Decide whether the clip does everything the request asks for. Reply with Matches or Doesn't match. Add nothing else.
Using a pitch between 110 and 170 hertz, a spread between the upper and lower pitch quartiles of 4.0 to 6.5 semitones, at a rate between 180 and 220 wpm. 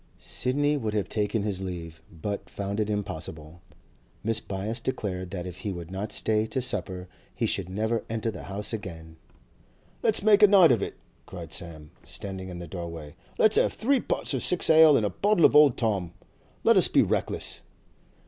Doesn't match